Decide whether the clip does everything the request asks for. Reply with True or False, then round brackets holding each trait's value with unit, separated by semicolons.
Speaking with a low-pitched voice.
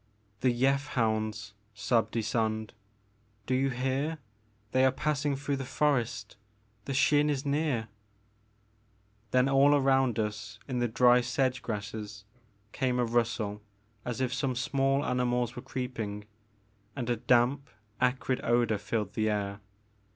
True (120 Hz)